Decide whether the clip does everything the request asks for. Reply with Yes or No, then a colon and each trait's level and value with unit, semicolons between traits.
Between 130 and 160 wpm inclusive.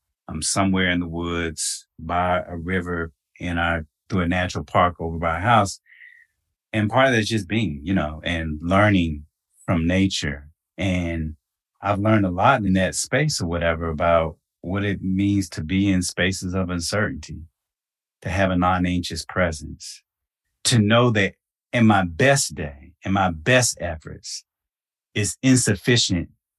Yes: average, 155 wpm